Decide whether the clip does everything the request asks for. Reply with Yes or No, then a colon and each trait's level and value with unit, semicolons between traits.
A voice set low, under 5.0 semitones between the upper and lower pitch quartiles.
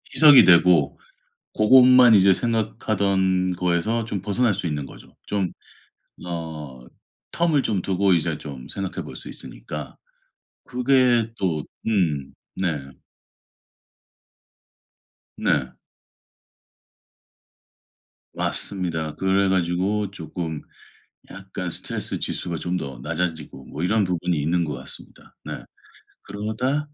Yes: very low, 95 Hz; average, 4.4 semitones